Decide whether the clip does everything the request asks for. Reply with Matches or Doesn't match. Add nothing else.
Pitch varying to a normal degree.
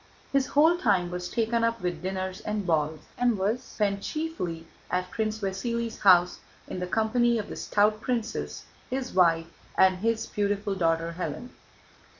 Matches